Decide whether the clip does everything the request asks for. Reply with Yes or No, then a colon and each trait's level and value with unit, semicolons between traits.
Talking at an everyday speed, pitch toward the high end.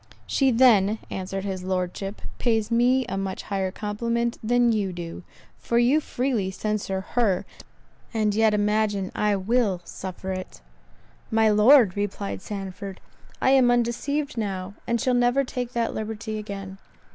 Yes: average, 145 wpm; high, 215 Hz